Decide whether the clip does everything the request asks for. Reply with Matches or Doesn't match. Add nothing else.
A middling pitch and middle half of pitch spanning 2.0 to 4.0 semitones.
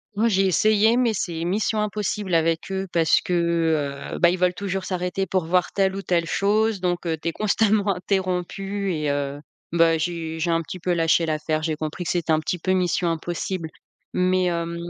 Matches